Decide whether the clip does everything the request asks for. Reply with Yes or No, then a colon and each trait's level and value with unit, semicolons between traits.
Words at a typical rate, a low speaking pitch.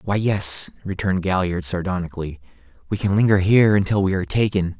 Yes: average, 165 wpm; very low, 95 Hz